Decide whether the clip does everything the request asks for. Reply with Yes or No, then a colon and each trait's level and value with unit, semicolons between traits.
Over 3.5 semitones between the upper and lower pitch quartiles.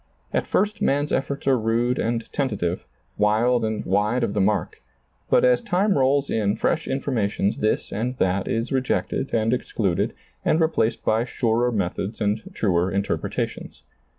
Yes: average, 3.9 semitones